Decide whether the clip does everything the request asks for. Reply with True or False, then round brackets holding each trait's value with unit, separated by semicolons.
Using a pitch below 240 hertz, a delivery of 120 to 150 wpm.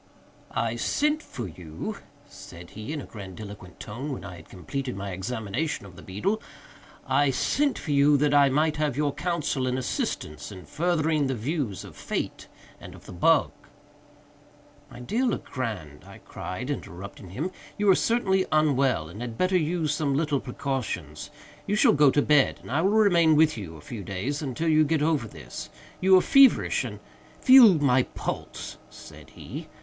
False (140 Hz; 175 wpm)